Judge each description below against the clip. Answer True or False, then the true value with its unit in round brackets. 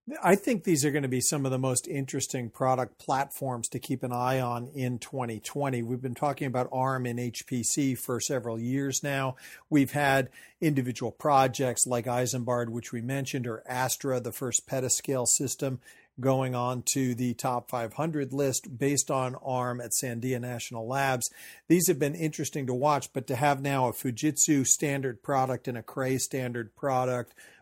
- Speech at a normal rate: True (175 wpm)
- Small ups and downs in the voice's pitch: True (2.0 semitones)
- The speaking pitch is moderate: False (130 Hz)